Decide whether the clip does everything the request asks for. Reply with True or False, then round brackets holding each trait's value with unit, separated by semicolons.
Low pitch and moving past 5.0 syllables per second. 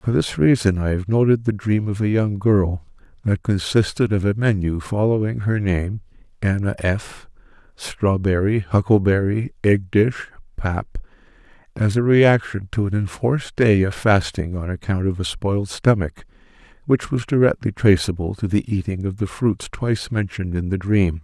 False (100 Hz; 4.5 syllables/s)